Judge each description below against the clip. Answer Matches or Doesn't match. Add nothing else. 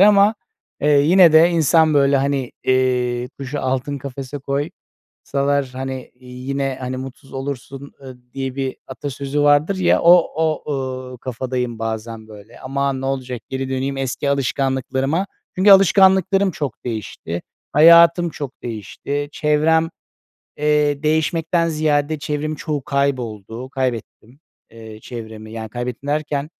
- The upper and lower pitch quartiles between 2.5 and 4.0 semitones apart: Matches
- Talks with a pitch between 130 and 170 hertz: Matches